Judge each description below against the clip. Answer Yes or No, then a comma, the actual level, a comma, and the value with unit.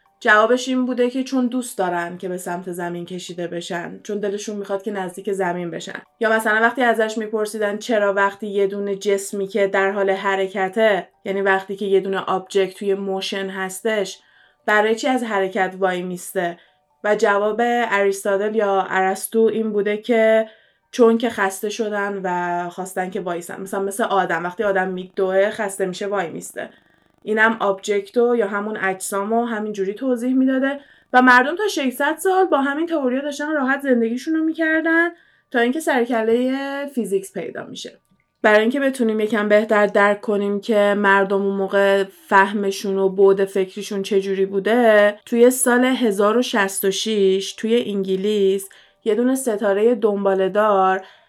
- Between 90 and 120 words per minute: No, average, 150 wpm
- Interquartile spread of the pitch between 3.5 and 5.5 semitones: No, average, 3.1 semitones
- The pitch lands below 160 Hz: No, high, 205 Hz